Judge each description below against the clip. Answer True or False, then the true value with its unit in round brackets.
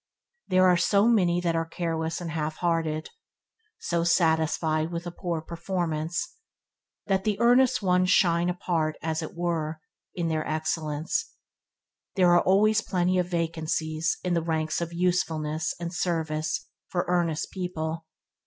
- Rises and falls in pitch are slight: True (2.1 semitones)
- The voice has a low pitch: False (170 Hz)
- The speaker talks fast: False (145 wpm)